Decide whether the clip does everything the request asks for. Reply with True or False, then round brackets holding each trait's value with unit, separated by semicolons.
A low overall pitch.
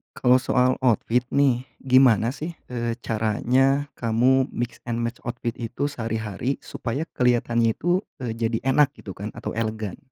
True (120 Hz)